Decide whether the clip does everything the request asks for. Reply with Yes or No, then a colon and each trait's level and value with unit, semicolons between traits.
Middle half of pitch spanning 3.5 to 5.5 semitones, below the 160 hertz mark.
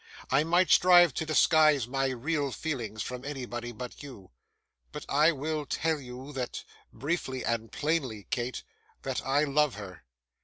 Yes: average, 3.8 semitones; low, 135 Hz